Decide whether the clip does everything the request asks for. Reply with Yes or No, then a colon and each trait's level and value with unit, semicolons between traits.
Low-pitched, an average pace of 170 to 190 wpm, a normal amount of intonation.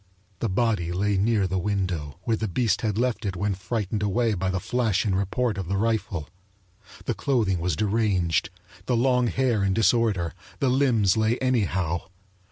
Yes: low, 105 Hz; average, 175 wpm; average, 3.7 semitones